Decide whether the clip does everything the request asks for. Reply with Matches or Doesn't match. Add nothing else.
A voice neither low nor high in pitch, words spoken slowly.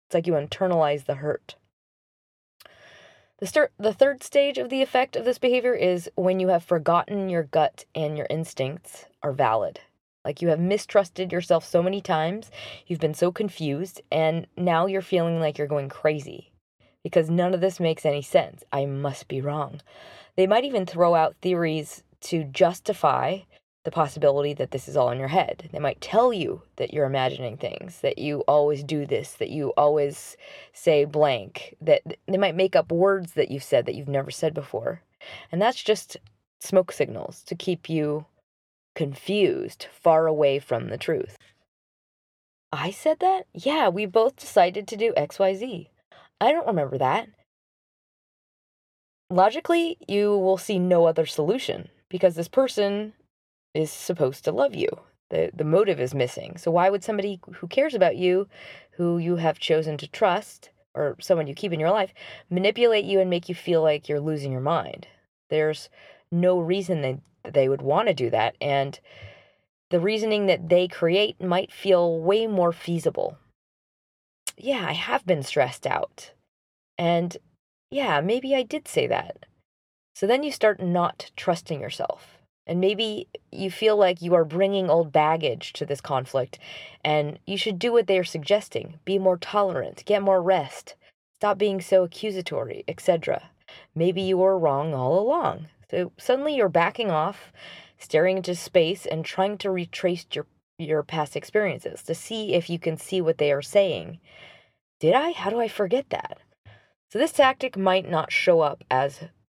Doesn't match